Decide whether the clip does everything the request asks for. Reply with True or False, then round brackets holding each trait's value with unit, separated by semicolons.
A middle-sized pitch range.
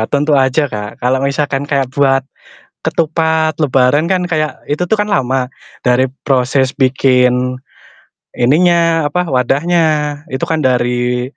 True (3.8 semitones)